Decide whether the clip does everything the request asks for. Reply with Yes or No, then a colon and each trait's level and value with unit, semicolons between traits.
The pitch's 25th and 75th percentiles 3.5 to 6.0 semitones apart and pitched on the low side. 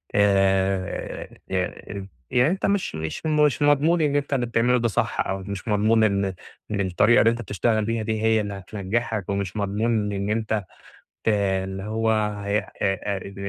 No: average, 2.8 semitones; low, 105 Hz